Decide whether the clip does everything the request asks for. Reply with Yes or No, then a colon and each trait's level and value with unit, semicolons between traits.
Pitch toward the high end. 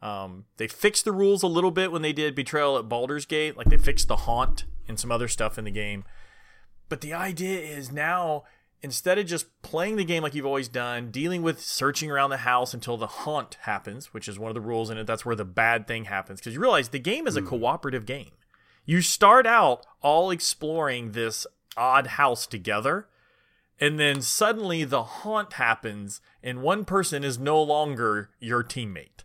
No: medium, 140 Hz